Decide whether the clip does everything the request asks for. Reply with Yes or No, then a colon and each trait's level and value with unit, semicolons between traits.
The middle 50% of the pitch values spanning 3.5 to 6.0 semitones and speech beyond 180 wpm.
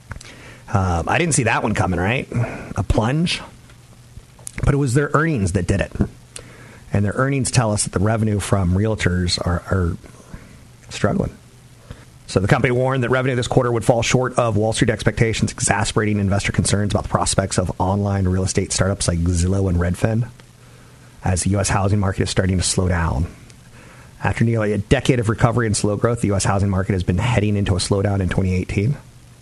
Yes: average, 4.0 semitones; average, 190 wpm